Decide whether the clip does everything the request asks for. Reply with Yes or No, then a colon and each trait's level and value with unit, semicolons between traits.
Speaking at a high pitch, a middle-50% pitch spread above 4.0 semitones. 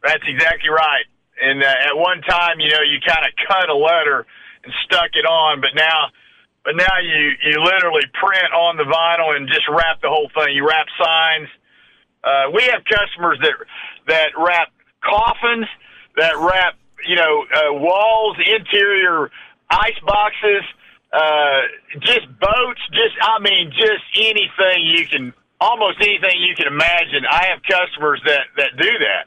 No: medium, 175 Hz; average, 5.2 semitones